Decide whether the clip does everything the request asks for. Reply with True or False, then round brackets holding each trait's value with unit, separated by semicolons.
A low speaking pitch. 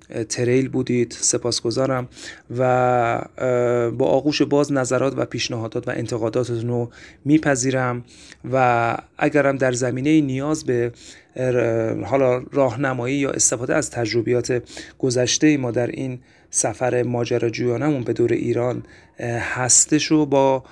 True (125 Hz)